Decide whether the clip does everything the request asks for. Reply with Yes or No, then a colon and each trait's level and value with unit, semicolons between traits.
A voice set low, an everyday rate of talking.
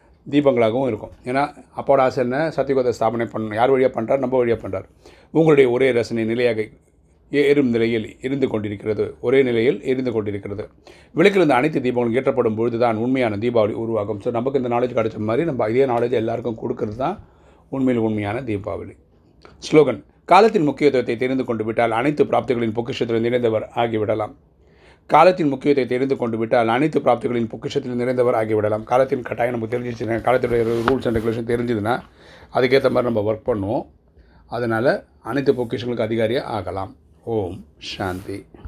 No: low, 120 Hz; fast, 145 wpm